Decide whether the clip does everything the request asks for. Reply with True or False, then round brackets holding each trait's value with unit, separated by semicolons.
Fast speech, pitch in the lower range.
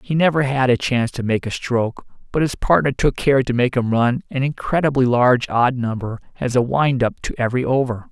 True (220 wpm; 125 Hz)